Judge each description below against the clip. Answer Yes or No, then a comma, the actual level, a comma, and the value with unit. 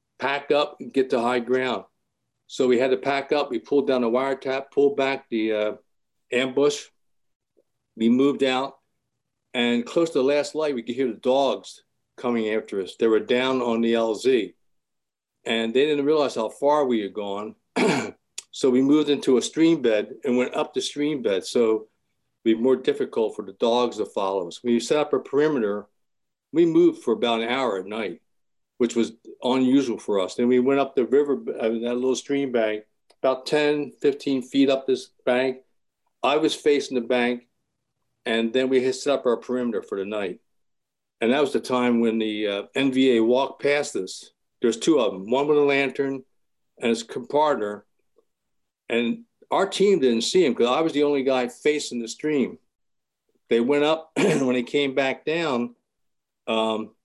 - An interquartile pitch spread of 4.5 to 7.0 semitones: No, average, 3.3 semitones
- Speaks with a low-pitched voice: Yes, low, 130 Hz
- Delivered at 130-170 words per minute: No, average, 190 wpm